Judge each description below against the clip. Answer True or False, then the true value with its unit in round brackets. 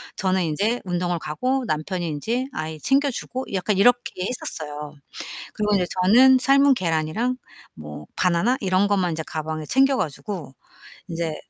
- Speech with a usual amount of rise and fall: False (7.6 semitones)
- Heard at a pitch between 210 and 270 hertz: False (185 Hz)